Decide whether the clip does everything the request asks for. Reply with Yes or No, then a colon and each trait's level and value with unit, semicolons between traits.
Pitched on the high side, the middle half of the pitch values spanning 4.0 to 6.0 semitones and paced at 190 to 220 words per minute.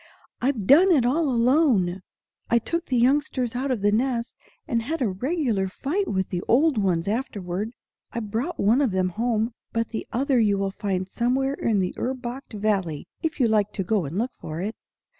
Yes: high, 230 Hz; average, 5.0 semitones; average, 195 wpm